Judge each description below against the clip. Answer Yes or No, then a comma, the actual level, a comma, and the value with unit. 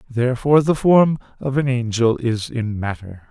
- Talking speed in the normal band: Yes, average, 165 wpm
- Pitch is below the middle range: Yes, low, 125 Hz